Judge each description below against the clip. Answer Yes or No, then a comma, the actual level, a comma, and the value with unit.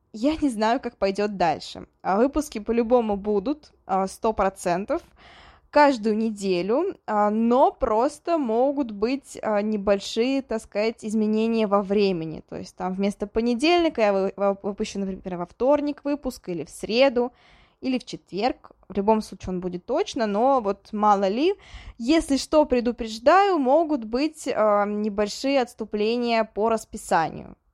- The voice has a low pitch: No, high, 225 Hz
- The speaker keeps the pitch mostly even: No, average, 4.7 semitones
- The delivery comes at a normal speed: Yes, average, 130 wpm